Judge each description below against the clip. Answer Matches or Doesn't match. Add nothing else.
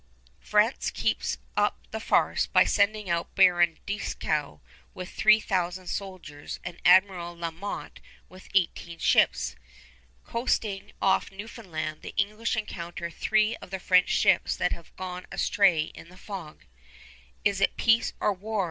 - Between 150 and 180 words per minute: Doesn't match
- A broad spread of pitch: Doesn't match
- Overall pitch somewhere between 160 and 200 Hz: Matches